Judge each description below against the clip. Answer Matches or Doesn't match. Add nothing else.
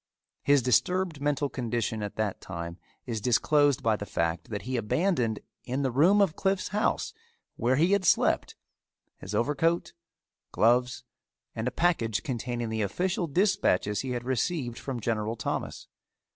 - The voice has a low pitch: Matches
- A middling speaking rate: Matches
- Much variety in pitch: Matches